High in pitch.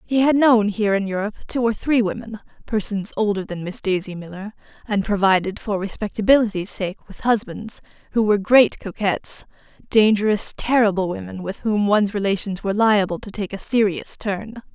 Yes: high, 205 Hz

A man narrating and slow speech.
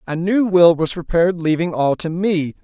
No: male; fast, 205 wpm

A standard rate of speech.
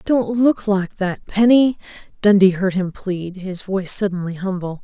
Yes: average, 160 wpm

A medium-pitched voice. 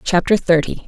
Yes: medium, 175 Hz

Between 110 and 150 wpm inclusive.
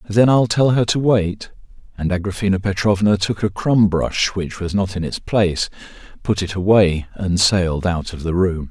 No: average, 195 wpm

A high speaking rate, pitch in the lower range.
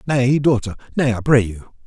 No: average, 195 wpm; low, 120 Hz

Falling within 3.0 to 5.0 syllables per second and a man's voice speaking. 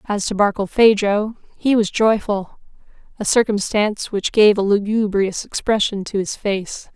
No: 4.5 syllables/s; female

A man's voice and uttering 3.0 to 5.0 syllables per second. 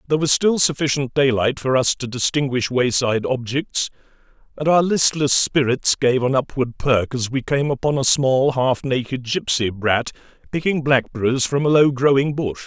Yes: male; 4.9 syllables/s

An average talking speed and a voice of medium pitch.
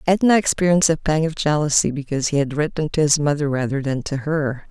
No: fast, 215 wpm; medium, 150 Hz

